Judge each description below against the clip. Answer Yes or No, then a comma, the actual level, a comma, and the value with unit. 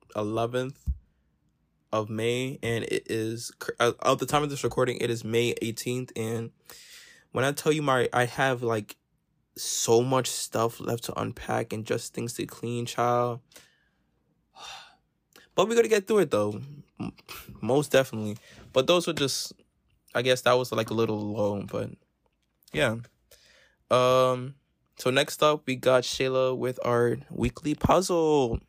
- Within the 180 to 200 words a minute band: No, average, 150 wpm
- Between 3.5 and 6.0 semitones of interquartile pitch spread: No, average, 2.8 semitones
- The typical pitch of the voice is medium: No, low, 125 Hz